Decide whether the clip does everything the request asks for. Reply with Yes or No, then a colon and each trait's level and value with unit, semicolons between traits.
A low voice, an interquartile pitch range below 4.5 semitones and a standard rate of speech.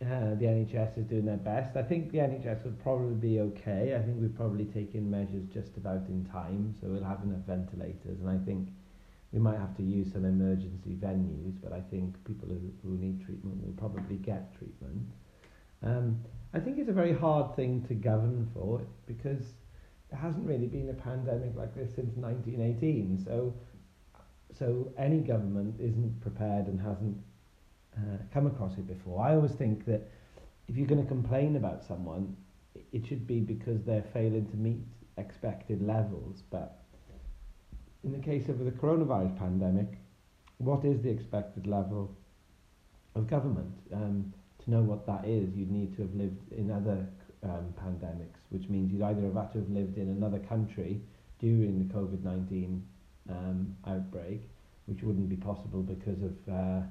Yes: low, 100 Hz; average, 3.5 semitones; average, 175 wpm